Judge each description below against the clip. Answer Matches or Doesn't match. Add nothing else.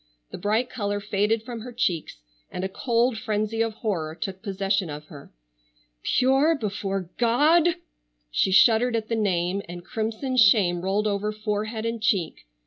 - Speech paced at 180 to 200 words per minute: Doesn't match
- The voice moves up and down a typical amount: Matches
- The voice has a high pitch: Matches